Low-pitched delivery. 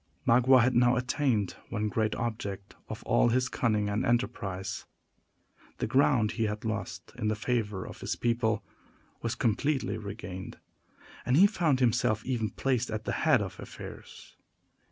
Yes: low, 115 Hz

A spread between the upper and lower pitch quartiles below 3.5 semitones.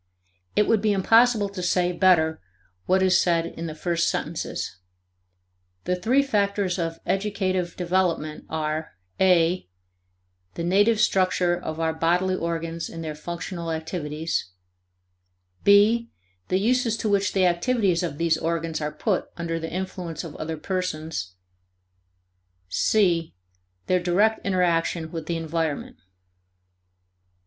Yes: average, 2.8 semitones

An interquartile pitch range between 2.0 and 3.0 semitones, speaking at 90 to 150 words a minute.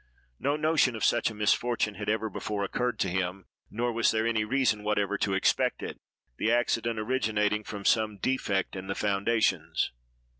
No: narrow, 2.4 semitones; average, 175 wpm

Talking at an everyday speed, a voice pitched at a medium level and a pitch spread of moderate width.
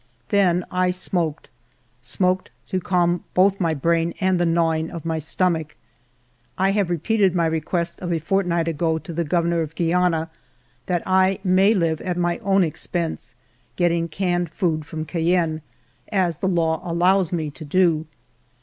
No: average, 160 wpm; medium, 170 Hz; narrow, 2.2 semitones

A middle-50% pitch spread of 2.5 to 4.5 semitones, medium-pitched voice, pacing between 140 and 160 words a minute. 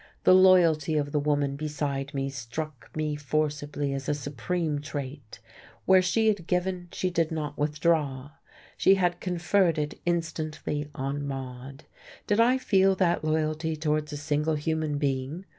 Yes: average, 3.1 semitones; medium, 155 Hz; average, 150 wpm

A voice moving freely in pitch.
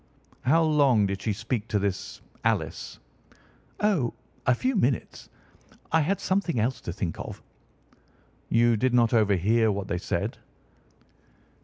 Yes: wide, 6.0 semitones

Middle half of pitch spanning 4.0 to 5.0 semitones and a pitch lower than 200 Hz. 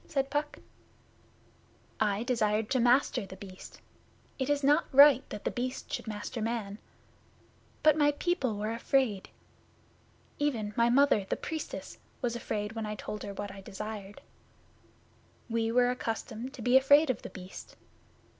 No: average, 4.4 semitones; high, 235 Hz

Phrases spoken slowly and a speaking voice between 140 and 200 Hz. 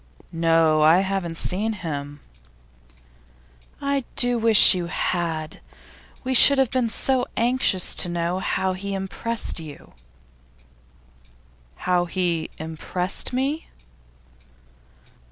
Yes: slow, 100 wpm; medium, 185 Hz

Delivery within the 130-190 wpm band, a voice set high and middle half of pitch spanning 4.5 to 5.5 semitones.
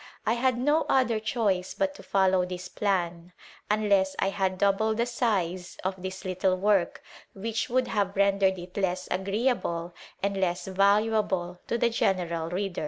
No: average, 160 wpm; high, 195 Hz; average, 3.0 semitones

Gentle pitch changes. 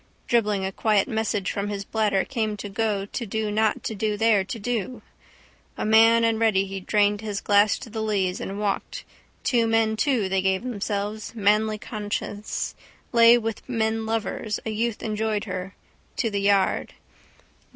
Yes: narrow, 1.8 semitones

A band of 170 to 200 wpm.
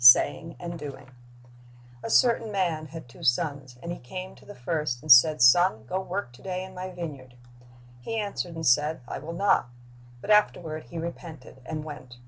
Yes: average, 190 wpm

